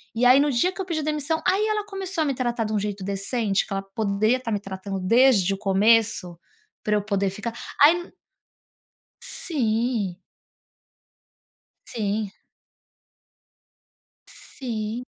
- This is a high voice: Yes, high, 225 Hz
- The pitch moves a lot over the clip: Yes, wide, 5.9 semitones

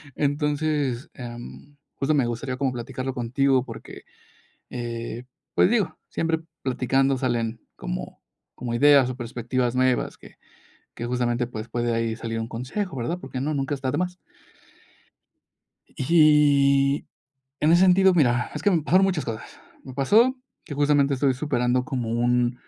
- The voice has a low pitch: Yes, low, 130 Hz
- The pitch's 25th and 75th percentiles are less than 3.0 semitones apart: No, average, 3.5 semitones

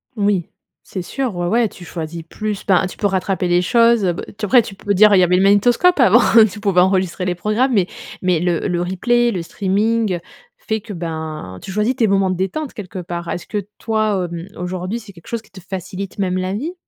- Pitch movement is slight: No, average, 3.3 semitones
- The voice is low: No, high, 195 Hz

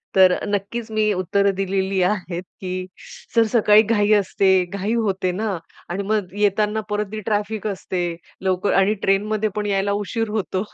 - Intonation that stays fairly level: Yes, narrow, 2.0 semitones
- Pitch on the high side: Yes, high, 200 Hz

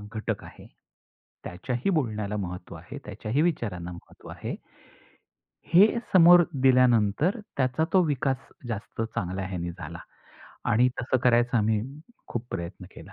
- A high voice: No, low, 115 Hz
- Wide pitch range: Yes, wide, 5.7 semitones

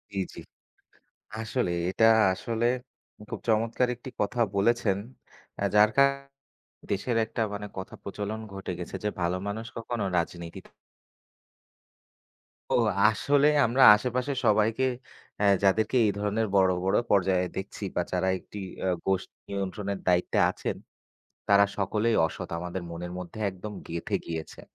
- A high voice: No, low, 100 Hz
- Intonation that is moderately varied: Yes, average, 3.2 semitones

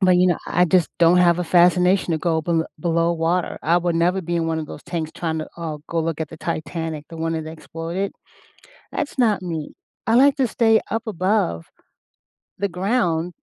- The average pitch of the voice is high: No, medium, 170 Hz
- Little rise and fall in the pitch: Yes, narrow, 2.2 semitones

